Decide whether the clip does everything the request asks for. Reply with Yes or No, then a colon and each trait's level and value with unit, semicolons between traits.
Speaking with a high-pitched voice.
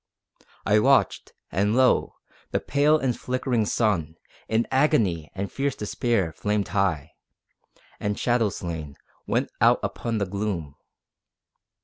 No: low, 105 Hz